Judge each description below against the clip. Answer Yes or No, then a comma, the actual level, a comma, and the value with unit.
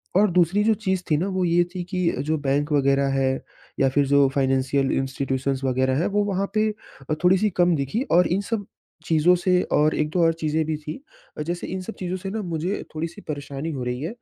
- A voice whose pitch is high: No, medium, 160 Hz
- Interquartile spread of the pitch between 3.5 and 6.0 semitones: Yes, average, 4.9 semitones